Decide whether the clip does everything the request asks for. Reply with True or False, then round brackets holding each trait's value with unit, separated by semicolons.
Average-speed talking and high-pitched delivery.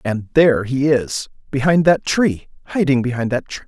False (145 wpm; 135 Hz)